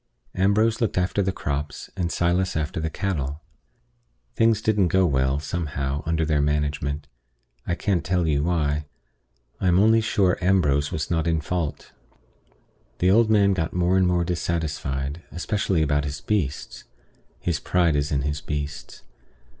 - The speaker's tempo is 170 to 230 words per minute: No, average, 155 wpm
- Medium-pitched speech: No, very low, 85 Hz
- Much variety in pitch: No, average, 4.2 semitones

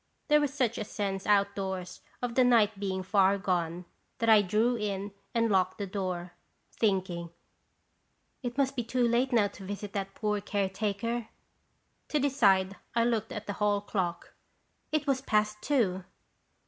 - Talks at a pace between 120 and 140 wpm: No, average, 160 wpm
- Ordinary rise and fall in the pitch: Yes, average, 3.4 semitones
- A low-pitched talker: No, high, 205 Hz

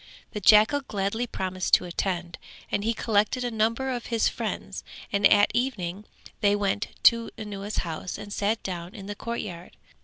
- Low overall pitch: No, high, 205 Hz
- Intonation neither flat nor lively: Yes, average, 3.0 semitones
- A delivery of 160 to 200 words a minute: Yes, average, 165 wpm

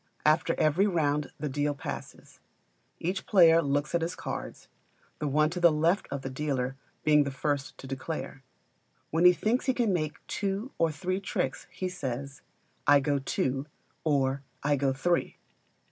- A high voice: No, medium, 150 Hz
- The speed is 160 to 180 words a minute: Yes, average, 165 wpm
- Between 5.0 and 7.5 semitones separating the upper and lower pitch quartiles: No, average, 3.8 semitones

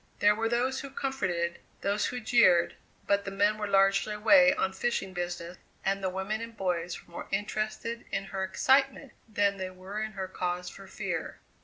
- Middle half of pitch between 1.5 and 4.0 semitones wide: Yes, average, 3.2 semitones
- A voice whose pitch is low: No, high, 200 Hz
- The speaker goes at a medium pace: Yes, average, 185 wpm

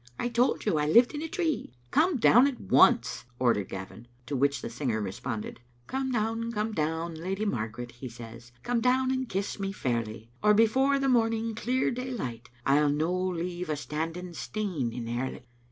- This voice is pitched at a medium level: Yes, medium, 180 Hz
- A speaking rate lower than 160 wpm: No, average, 185 wpm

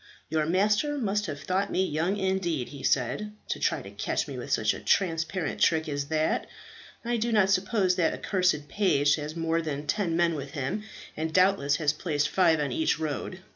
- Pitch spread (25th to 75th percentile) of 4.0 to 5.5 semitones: Yes, average, 4.3 semitones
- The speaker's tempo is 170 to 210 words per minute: Yes, average, 195 wpm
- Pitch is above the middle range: No, medium, 165 Hz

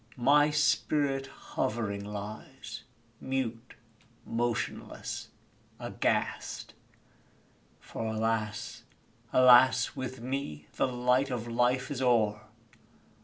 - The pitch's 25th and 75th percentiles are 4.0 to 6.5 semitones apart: No, average, 2.8 semitones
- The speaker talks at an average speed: No, slow, 80 wpm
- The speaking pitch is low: Yes, low, 120 Hz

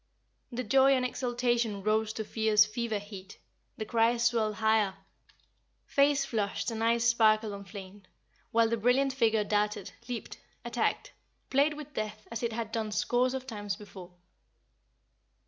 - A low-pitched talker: No, high, 225 Hz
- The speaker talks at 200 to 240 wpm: No, average, 145 wpm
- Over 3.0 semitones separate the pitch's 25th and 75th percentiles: No, narrow, 2.4 semitones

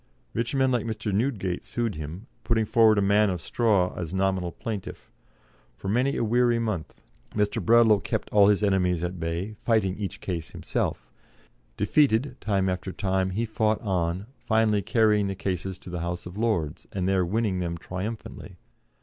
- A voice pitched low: Yes, low, 100 Hz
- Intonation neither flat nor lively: Yes, average, 3.5 semitones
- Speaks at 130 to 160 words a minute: No, average, 170 wpm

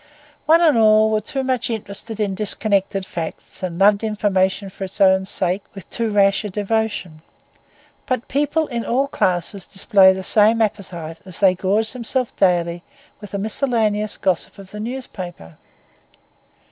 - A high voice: Yes, high, 205 Hz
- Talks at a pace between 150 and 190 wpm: Yes, average, 155 wpm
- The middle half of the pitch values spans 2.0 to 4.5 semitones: Yes, average, 2.9 semitones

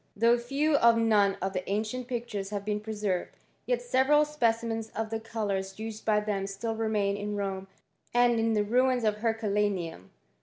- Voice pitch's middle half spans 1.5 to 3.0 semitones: Yes, narrow, 2.4 semitones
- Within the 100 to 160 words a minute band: No, average, 175 wpm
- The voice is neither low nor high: No, high, 220 Hz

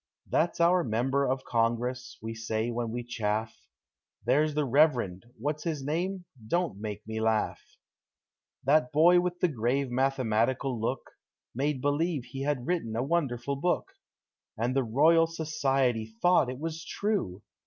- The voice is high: No, low, 135 Hz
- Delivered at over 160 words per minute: No, average, 155 wpm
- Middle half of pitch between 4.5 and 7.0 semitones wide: Yes, average, 5.2 semitones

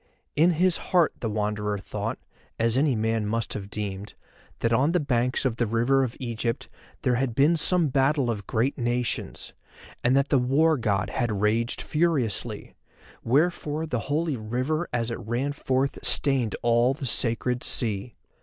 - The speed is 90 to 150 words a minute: No, average, 165 wpm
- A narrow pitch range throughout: No, average, 3.9 semitones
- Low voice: Yes, low, 125 Hz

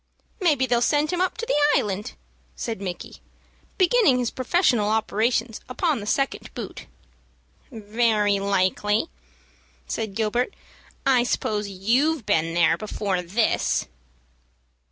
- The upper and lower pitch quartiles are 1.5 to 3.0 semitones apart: No, average, 4.7 semitones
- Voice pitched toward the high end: Yes, high, 225 Hz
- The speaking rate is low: Yes, slow, 115 wpm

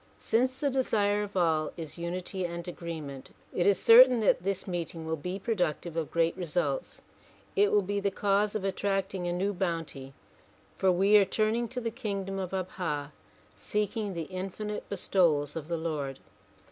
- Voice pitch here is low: No, medium, 185 Hz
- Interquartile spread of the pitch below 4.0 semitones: Yes, average, 3.5 semitones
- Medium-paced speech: Yes, average, 170 wpm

